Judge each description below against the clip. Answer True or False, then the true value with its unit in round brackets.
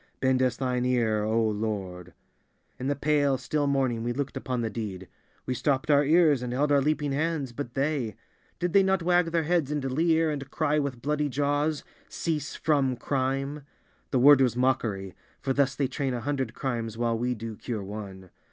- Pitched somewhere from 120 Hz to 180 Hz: True (135 Hz)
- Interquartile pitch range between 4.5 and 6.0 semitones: False (3.7 semitones)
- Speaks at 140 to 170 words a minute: False (185 wpm)